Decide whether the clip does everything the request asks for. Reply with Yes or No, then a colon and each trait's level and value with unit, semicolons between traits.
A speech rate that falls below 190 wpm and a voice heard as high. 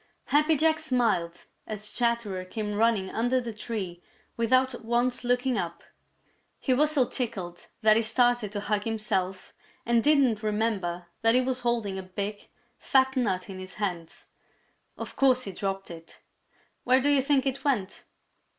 Yes: average, 160 wpm; high, 225 Hz